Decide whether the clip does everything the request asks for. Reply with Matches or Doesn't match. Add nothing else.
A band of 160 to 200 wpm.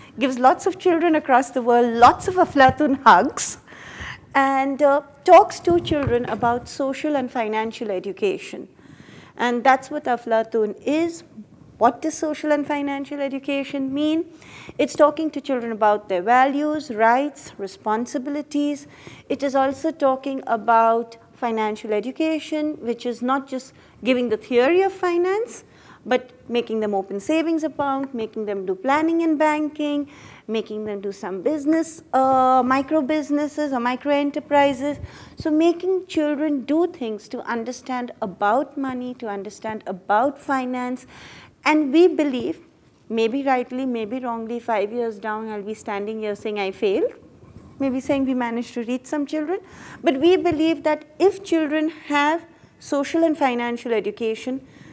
Doesn't match